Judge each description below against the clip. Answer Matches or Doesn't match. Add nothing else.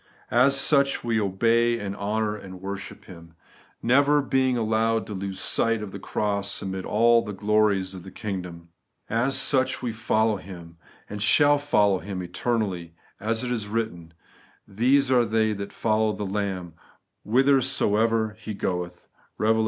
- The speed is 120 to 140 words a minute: Doesn't match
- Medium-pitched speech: Doesn't match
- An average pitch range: Matches